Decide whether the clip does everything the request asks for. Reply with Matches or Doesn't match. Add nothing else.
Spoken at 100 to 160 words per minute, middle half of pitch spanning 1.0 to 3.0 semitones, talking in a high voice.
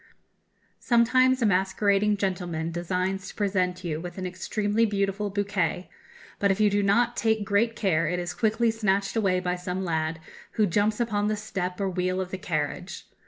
Doesn't match